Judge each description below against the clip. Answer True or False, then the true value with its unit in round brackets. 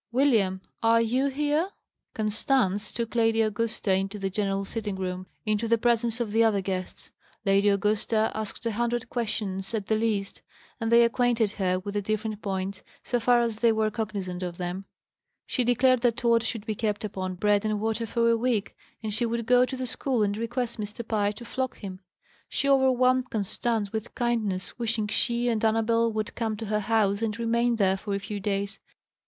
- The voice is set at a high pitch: True (220 Hz)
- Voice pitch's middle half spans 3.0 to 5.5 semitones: False (2.6 semitones)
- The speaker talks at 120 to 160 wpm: False (195 wpm)